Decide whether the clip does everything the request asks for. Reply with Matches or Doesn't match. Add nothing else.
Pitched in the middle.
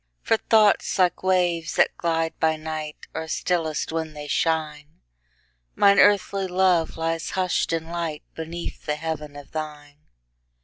Matches